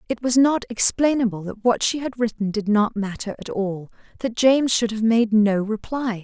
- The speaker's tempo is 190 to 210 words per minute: Yes, average, 200 wpm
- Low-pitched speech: No, high, 225 Hz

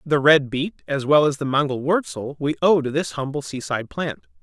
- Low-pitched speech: No, medium, 145 Hz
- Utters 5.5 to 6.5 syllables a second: No, 5.3 syllables/s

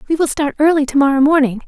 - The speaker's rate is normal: No, fast, 250 wpm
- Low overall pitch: No, very high, 285 Hz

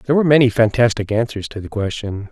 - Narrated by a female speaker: No, male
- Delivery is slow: No, fast, 205 wpm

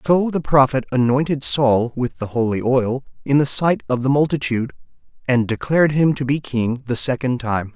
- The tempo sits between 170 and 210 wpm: Yes, average, 185 wpm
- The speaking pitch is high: No, low, 130 Hz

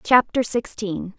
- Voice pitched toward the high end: Yes, high, 220 Hz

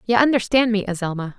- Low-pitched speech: No, high, 215 Hz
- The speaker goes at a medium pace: Yes, average, 175 wpm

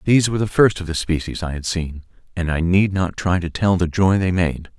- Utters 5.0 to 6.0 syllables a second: Yes, 5.6 syllables/s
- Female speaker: No, male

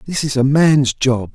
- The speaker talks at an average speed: No, fast, 225 wpm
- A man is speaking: Yes, male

